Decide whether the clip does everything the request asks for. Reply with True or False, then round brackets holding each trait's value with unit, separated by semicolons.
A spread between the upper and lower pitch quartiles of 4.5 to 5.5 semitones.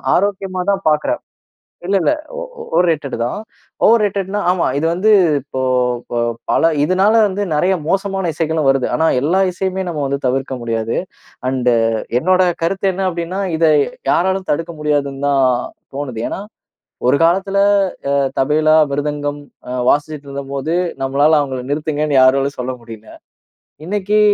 True (5.2 semitones)